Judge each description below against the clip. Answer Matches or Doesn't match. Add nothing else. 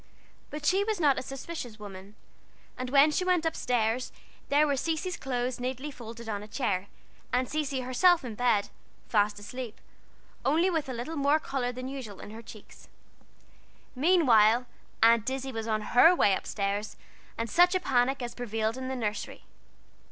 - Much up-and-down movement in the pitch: Doesn't match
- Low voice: Doesn't match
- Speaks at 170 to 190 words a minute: Matches